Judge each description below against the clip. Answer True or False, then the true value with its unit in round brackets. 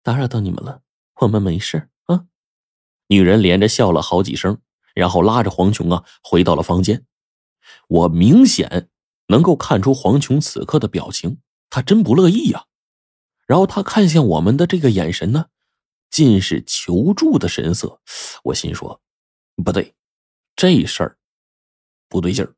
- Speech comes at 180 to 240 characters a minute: True (225 characters per minute)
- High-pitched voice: False (115 Hz)